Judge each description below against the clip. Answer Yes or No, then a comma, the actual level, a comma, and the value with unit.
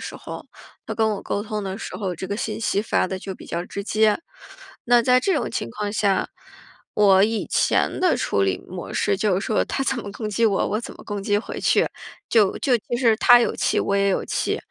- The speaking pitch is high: Yes, high, 210 Hz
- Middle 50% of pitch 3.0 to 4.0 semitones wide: No, narrow, 2.5 semitones